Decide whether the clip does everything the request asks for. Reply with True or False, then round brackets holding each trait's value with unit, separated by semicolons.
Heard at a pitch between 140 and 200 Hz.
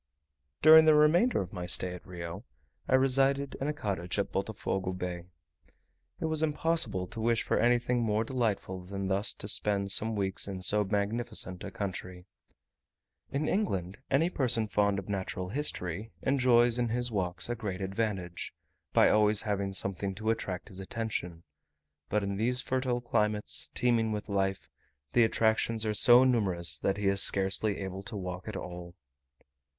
False (105 Hz)